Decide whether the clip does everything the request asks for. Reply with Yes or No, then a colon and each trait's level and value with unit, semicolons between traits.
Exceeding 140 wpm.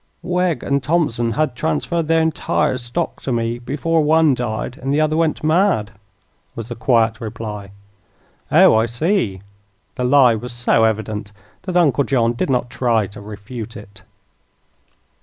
Yes: average, 155 wpm